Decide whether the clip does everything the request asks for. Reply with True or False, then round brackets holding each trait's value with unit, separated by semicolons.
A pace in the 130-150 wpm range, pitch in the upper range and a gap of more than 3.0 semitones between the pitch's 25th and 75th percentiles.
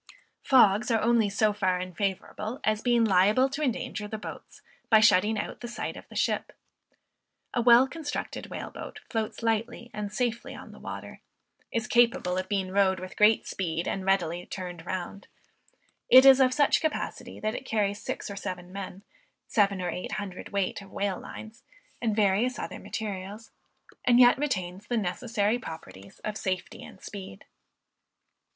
False (165 wpm; 210 Hz; 3.9 semitones)